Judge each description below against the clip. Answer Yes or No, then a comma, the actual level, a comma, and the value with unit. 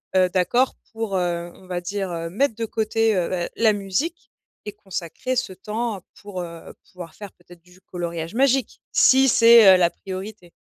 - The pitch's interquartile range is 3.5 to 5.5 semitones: Yes, average, 4.1 semitones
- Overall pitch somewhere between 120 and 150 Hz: No, high, 195 Hz